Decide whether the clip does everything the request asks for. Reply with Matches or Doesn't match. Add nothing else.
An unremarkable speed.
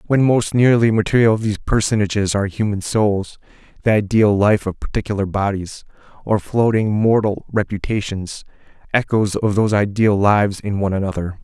Doesn't match